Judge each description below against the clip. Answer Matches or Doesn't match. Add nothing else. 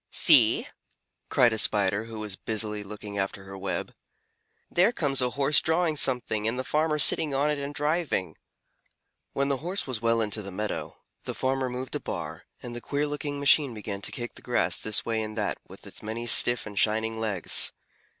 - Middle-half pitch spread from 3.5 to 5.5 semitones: Matches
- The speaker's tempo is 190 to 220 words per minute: Matches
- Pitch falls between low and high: Doesn't match